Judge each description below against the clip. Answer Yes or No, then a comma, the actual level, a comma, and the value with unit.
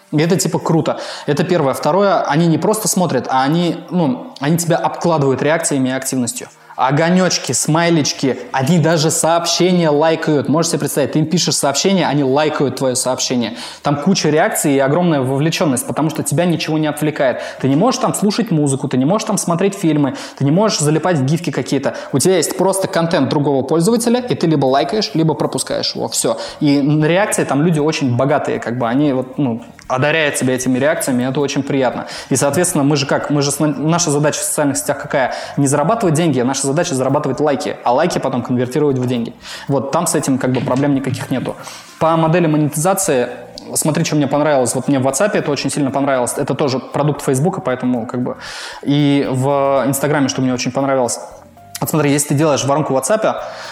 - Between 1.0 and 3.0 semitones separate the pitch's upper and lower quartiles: No, average, 3.5 semitones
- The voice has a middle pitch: Yes, medium, 145 Hz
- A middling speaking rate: No, fast, 195 wpm